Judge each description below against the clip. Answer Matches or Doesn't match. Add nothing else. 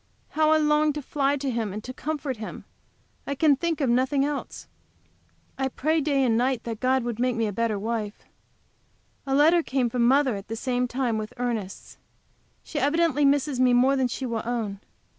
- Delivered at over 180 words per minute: Matches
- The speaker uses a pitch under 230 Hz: Doesn't match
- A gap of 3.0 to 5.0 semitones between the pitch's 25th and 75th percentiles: Matches